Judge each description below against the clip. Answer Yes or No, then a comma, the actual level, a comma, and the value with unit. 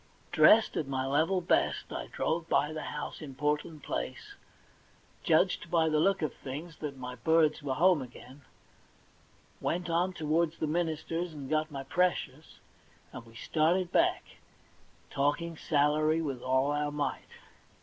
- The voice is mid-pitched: Yes, medium, 155 Hz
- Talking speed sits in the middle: Yes, average, 150 wpm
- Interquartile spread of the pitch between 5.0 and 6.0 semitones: No, average, 2.9 semitones